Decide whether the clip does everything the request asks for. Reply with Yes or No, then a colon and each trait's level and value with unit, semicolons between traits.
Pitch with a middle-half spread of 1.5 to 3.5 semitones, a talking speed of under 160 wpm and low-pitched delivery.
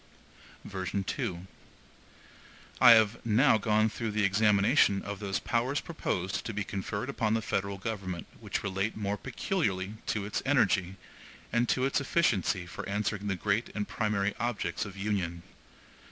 Yes: narrow, 2.5 semitones; average, 145 wpm; low, 105 Hz